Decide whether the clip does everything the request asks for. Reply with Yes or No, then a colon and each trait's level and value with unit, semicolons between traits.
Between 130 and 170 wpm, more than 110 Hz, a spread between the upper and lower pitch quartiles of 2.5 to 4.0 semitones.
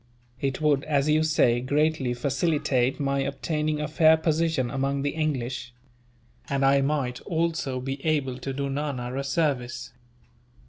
Yes: average, 145 wpm; medium, 140 Hz; average, 2.8 semitones